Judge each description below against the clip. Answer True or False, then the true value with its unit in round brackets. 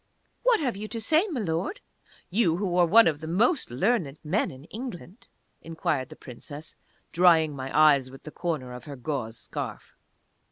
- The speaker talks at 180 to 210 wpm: False (170 wpm)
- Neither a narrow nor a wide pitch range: False (7.0 semitones)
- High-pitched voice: False (165 Hz)